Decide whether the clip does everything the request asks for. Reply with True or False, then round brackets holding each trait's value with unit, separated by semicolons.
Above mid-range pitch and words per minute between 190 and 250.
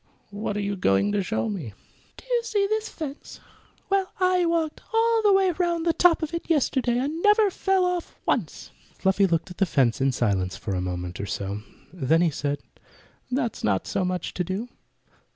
True (230 Hz; 200 wpm)